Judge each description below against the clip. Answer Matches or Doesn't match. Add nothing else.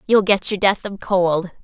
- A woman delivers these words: Matches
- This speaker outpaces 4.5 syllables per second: Doesn't match